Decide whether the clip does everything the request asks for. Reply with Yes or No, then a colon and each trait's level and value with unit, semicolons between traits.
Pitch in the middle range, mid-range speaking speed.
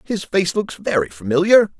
Yes: medium, 175 Hz; average, 170 wpm